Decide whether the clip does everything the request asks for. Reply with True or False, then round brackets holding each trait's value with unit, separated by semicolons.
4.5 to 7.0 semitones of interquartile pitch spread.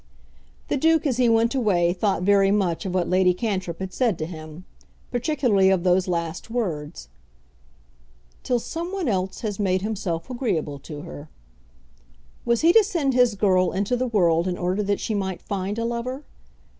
True (4.9 semitones)